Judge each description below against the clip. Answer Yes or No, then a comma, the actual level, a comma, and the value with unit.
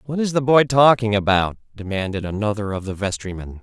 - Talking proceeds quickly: No, average, 180 wpm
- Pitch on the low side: Yes, low, 110 Hz